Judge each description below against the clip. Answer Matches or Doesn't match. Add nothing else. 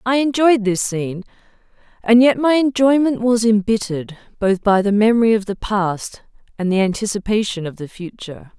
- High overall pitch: Matches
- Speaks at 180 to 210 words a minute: Doesn't match